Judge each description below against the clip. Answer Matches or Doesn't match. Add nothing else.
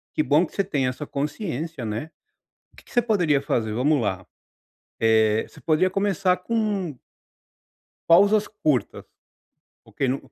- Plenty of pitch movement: Matches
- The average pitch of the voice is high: Doesn't match